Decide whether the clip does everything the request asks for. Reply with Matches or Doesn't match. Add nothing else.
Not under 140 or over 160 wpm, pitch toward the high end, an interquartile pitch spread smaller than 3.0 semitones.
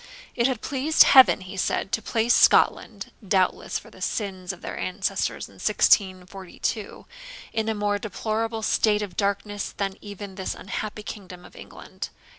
Matches